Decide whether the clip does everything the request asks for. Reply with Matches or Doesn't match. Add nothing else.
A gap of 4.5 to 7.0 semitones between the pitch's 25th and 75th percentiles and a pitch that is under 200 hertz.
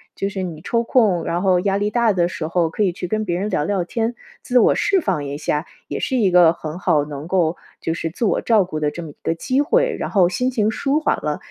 Matches